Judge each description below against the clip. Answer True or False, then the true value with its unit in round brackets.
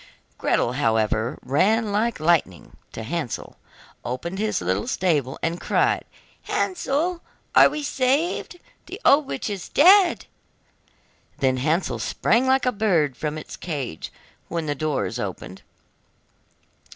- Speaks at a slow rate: True (125 wpm)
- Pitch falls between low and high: True (170 Hz)